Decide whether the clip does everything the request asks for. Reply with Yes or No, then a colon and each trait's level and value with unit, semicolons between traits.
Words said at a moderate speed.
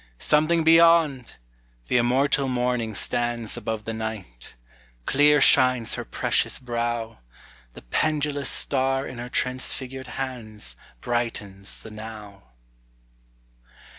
No: slow, 105 wpm